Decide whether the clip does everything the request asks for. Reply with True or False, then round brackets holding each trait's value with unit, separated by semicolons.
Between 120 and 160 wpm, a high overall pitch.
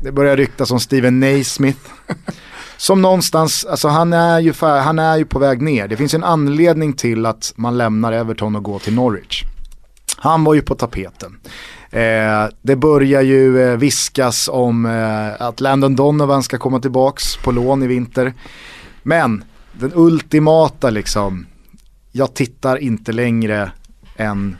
False (150 wpm; 130 Hz)